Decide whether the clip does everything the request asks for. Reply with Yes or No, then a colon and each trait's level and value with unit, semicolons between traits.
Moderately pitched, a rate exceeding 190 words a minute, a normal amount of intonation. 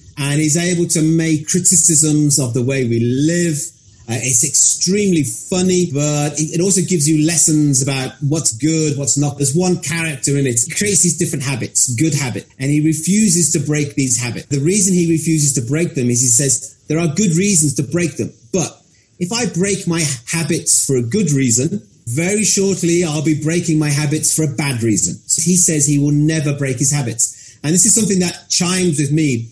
Yes: medium, 155 Hz; fast, 205 wpm; average, 3.7 semitones